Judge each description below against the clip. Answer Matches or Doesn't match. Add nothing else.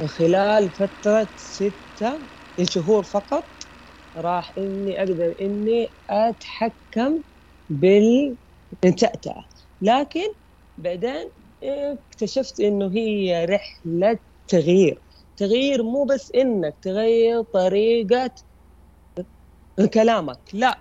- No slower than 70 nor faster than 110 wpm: Matches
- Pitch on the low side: Doesn't match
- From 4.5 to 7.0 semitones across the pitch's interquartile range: Doesn't match